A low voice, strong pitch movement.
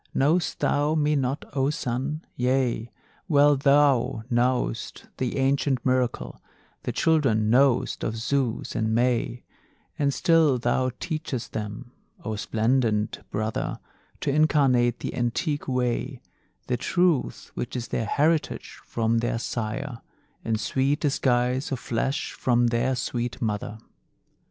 No: low, 125 Hz; average, 3.2 semitones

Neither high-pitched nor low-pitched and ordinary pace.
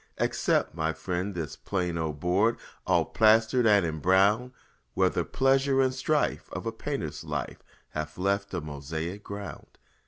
No: low, 100 Hz; average, 150 wpm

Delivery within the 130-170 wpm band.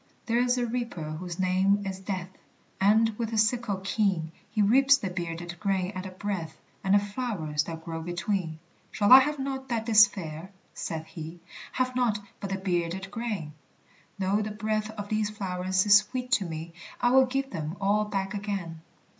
No: average, 185 wpm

